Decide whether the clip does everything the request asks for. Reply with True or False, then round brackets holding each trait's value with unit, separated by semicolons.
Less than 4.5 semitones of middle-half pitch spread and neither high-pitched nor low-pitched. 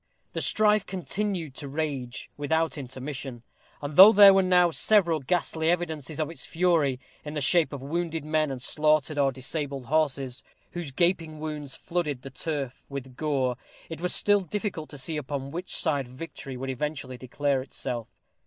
True (3.8 semitones; 150 Hz)